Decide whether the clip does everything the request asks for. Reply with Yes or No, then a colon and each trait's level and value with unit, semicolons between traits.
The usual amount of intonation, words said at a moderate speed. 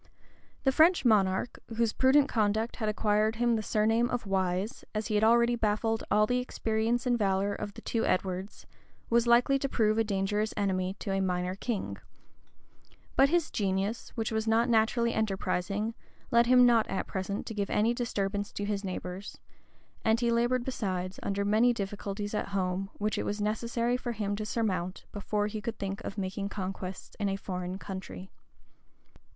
Yes: average, 3.1 semitones; average, 175 wpm